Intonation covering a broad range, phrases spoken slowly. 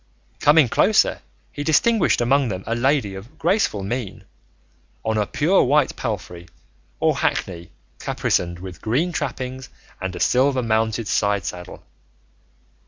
Yes: wide, 6.4 semitones; slow, 130 wpm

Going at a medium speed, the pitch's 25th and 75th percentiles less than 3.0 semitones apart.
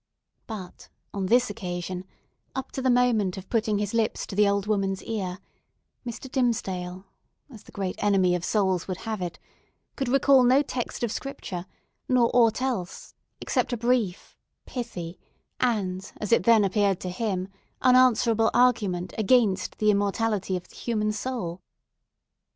No: average, 150 wpm; average, 4.3 semitones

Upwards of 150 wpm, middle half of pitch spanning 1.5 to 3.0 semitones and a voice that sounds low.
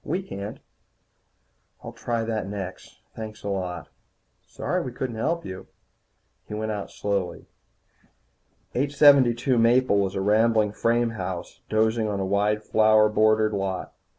No: slow, 135 wpm; narrow, 2.6 semitones; low, 110 Hz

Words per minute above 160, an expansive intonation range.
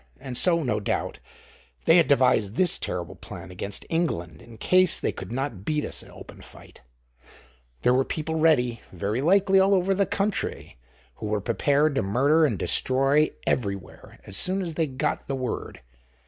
Yes: average, 175 wpm; wide, 7.4 semitones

